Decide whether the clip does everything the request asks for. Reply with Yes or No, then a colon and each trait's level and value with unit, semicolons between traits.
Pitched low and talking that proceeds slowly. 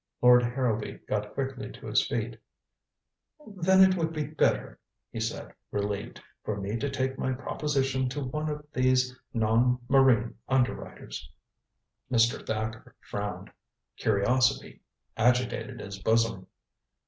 Yes: low, 125 Hz; slow, 125 wpm